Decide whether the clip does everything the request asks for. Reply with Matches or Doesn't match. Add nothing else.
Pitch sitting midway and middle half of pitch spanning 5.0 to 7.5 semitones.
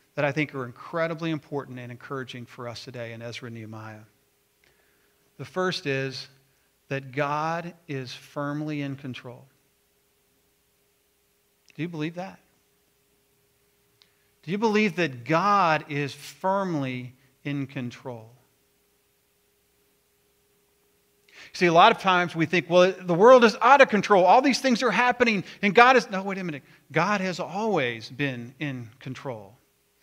Matches